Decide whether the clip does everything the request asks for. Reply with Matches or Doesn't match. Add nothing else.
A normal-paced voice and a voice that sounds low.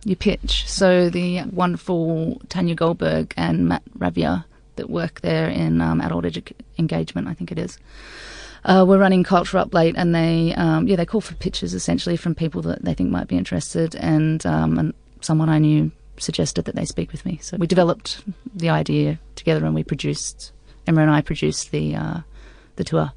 Doesn't match